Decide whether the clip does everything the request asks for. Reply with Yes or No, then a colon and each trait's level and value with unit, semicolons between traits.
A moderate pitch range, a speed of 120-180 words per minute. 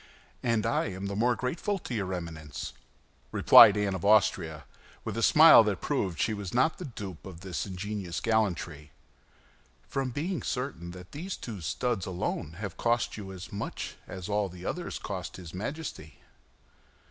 Yes: average, 4.8 semitones; average, 165 wpm